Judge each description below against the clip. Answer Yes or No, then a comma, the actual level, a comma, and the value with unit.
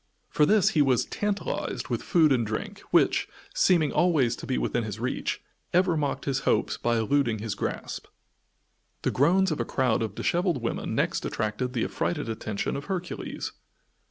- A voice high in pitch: No, low, 135 Hz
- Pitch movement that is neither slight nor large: No, wide, 6.8 semitones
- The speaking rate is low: No, average, 170 wpm